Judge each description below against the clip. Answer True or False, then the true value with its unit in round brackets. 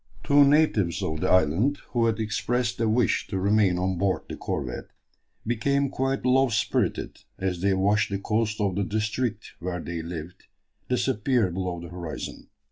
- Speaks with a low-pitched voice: True (105 Hz)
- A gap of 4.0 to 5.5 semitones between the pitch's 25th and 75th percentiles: True (4.8 semitones)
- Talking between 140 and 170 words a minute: True (165 wpm)